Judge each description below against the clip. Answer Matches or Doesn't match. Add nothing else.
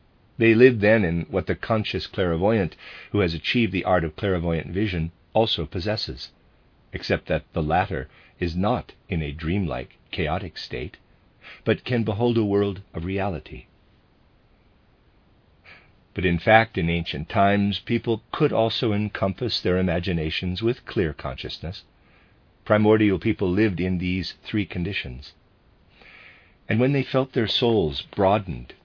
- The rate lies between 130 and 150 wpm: Matches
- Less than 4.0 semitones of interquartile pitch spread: Doesn't match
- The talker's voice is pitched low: Matches